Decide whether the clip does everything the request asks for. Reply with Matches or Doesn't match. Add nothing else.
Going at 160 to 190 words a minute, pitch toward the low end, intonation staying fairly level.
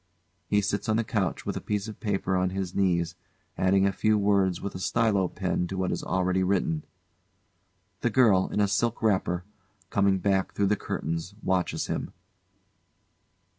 Matches